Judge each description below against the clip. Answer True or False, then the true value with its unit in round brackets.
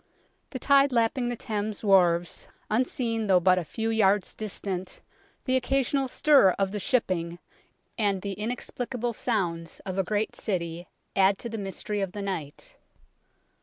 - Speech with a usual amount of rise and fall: True (4.1 semitones)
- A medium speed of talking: True (150 wpm)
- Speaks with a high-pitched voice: True (205 Hz)